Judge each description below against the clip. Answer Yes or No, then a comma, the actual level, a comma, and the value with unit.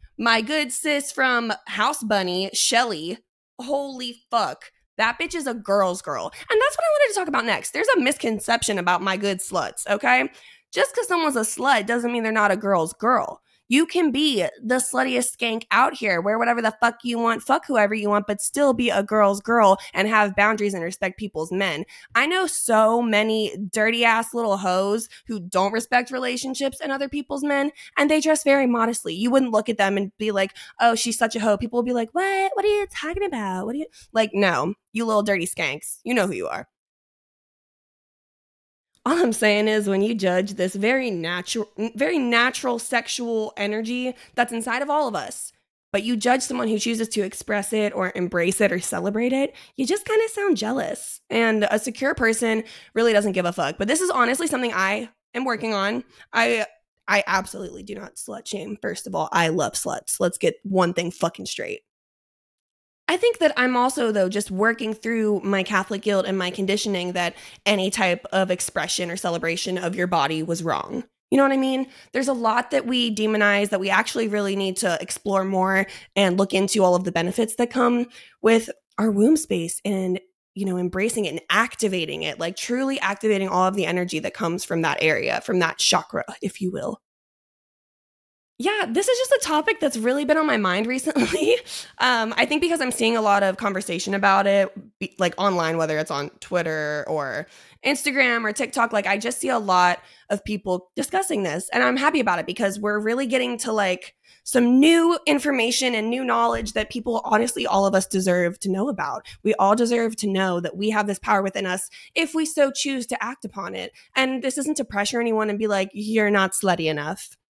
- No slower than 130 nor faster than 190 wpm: No, fast, 205 wpm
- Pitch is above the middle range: Yes, high, 220 Hz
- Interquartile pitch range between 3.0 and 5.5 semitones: Yes, average, 4.6 semitones